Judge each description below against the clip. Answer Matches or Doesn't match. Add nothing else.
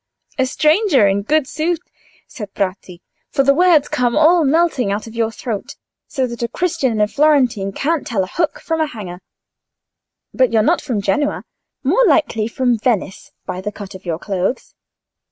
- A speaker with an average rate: Matches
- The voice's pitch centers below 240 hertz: Doesn't match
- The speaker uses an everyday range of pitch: Doesn't match